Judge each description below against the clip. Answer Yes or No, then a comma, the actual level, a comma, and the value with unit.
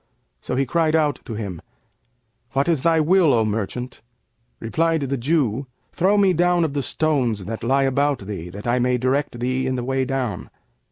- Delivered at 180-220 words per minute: Yes, average, 185 wpm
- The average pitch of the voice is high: No, low, 135 Hz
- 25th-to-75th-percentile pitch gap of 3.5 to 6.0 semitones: Yes, average, 4.7 semitones